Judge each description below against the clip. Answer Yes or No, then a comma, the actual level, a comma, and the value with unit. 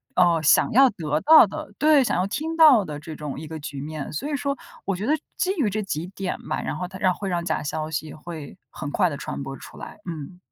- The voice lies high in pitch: No, medium, 175 Hz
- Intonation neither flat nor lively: No, wide, 5.8 semitones